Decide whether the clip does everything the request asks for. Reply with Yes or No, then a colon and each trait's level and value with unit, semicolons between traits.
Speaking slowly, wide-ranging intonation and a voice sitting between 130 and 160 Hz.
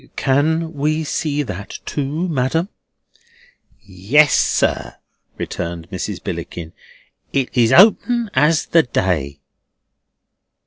Yes: slow, 95 wpm; wide, 8.5 semitones; medium, 140 Hz